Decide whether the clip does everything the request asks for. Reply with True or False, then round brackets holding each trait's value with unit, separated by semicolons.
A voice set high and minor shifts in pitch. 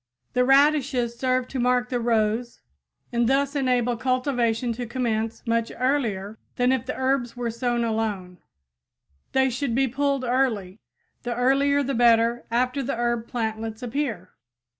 True (245 Hz; 2.3 semitones)